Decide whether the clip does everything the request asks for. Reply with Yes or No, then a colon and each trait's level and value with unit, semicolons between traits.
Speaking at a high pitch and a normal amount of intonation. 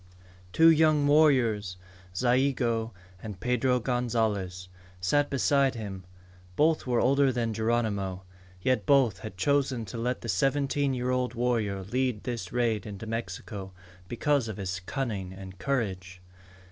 No: low, 120 Hz; average, 4.6 semitones